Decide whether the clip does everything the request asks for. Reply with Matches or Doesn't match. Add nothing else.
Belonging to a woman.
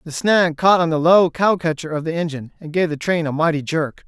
Doesn't match